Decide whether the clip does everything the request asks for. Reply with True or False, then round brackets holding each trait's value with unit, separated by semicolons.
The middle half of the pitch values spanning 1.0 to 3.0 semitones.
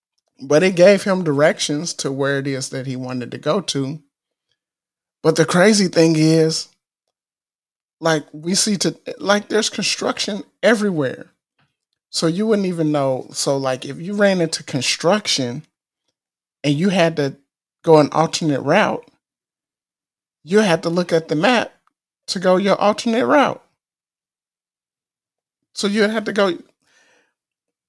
False (5.4 semitones)